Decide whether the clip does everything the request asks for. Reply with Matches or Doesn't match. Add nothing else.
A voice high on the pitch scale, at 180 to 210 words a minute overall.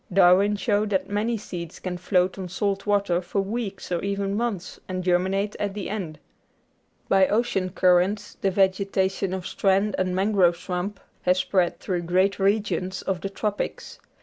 Doesn't match